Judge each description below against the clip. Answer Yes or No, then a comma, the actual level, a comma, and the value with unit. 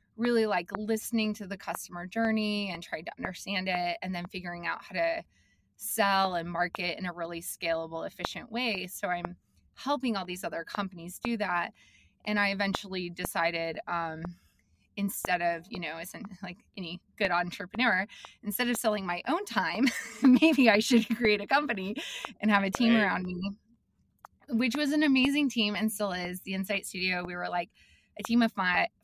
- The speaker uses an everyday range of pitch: Yes, average, 4.3 semitones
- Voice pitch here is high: Yes, high, 195 Hz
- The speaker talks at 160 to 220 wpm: Yes, average, 180 wpm